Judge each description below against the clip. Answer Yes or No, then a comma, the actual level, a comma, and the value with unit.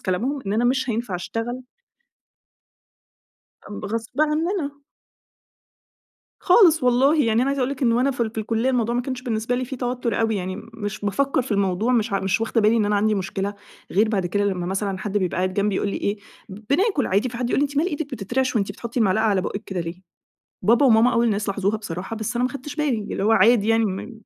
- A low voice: No, high, 225 Hz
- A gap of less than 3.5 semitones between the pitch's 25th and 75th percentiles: No, average, 4.0 semitones